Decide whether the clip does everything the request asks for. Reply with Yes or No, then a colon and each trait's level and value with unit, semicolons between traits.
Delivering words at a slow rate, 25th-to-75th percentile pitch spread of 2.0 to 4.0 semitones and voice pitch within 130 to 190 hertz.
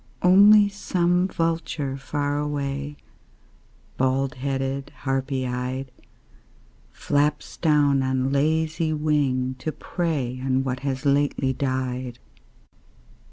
Yes: slow, 95 wpm; average, 2.7 semitones; medium, 140 Hz